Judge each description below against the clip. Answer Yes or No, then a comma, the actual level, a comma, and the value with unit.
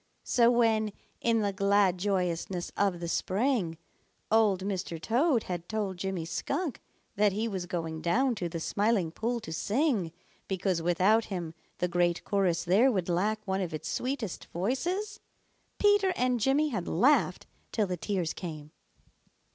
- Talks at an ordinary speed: Yes, average, 155 wpm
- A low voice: No, high, 195 Hz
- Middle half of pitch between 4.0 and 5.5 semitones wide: Yes, average, 4.8 semitones